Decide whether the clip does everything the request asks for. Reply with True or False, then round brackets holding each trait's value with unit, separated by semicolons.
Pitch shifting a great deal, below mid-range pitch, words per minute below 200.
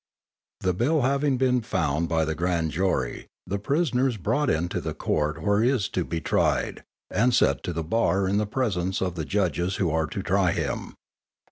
False (6.6 semitones; 95 Hz; 205 wpm)